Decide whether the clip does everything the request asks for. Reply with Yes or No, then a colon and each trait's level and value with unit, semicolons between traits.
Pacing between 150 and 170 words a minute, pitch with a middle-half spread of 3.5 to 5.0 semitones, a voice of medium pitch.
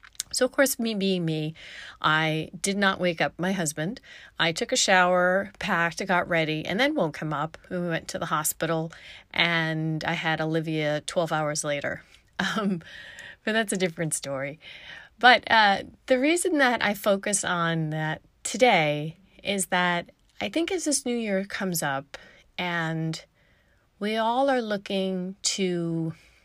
Yes: average, 155 wpm; average, 4.6 semitones; medium, 180 Hz